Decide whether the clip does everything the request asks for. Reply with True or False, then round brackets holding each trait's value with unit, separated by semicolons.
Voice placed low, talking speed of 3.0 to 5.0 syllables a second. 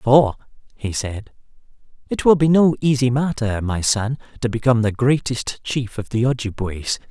True (120 Hz; 4.7 syllables/s)